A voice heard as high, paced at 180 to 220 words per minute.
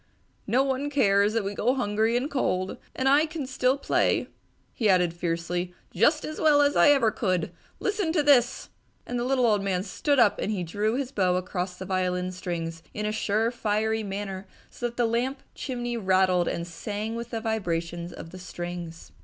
Yes: high, 215 Hz; average, 190 wpm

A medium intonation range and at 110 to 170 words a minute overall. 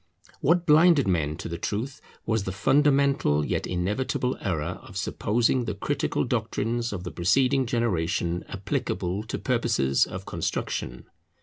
No: wide, 6.6 semitones; slow, 135 wpm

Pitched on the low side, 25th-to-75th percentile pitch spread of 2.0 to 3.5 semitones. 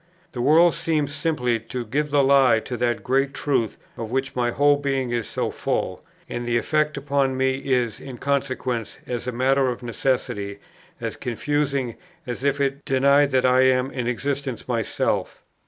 Yes: low, 130 Hz; narrow, 2.4 semitones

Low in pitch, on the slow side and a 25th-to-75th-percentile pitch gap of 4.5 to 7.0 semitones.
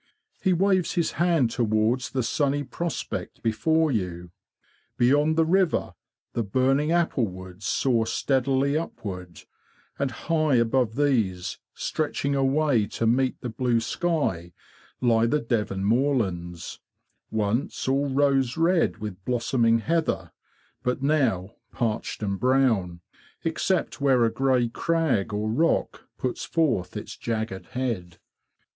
Yes: low, 125 Hz; slow, 125 wpm; average, 4.9 semitones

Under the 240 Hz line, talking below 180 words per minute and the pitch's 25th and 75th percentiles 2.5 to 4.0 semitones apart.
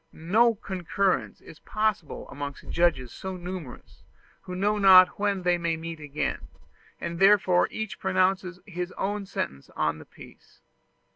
Yes: medium, 185 Hz; average, 140 wpm; average, 2.8 semitones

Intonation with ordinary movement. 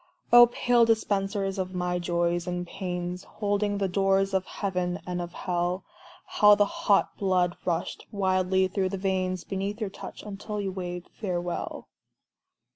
No: narrow, 2.1 semitones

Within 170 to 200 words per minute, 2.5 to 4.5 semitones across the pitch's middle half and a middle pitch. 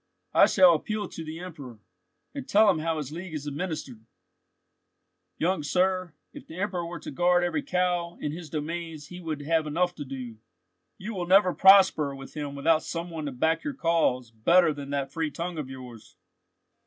Yes: average, 190 wpm; average, 3.6 semitones; medium, 165 Hz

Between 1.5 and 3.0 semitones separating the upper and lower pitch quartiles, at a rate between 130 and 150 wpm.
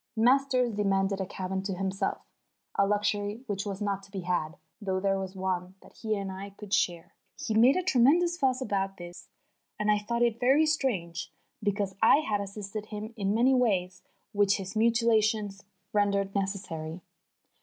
No: average, 2.7 semitones; average, 175 wpm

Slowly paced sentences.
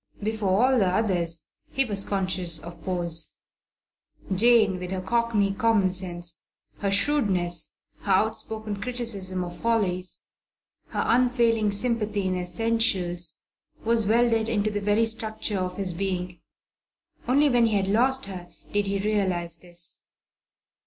Yes: slow, 130 wpm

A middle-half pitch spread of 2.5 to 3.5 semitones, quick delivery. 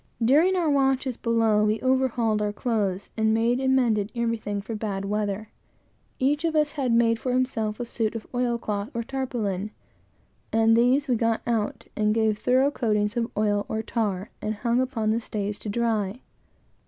No: average, 3.0 semitones; average, 180 wpm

